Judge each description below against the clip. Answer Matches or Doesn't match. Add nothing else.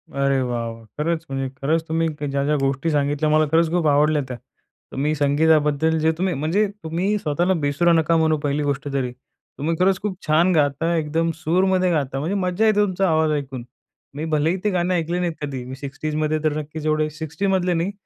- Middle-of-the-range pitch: Matches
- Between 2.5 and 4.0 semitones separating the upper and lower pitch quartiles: Matches